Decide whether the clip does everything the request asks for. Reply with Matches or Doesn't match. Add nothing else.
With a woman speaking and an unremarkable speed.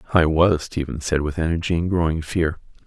Doesn't match